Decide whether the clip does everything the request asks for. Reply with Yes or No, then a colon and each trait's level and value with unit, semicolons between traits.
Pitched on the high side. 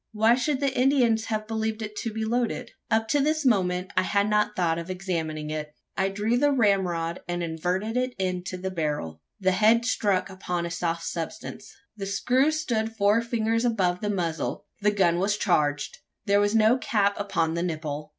Yes: high, 200 Hz